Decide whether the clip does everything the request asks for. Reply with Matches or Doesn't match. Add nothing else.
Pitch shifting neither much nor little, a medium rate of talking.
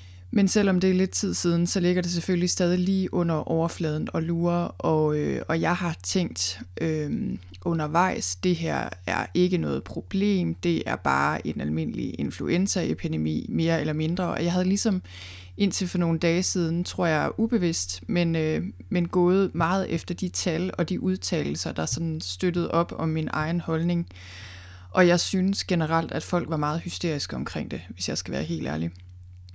Matches